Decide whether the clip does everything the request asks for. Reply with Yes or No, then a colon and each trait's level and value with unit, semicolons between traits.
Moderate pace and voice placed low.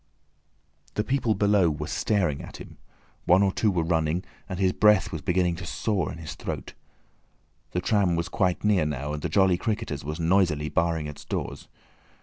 Yes: average, 180 wpm; very low, 90 Hz